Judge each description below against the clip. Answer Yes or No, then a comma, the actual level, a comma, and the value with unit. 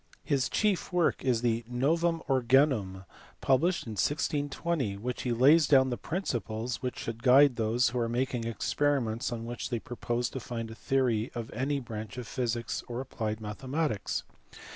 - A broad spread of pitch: No, average, 3.2 semitones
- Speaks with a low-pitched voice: Yes, low, 125 Hz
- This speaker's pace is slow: No, average, 165 wpm